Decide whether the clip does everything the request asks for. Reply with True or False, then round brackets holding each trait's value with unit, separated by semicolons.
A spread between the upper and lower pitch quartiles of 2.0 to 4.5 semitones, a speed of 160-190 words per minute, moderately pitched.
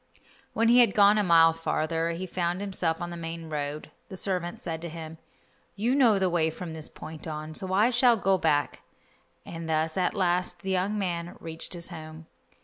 False (2.8 semitones; 200 wpm; 170 Hz)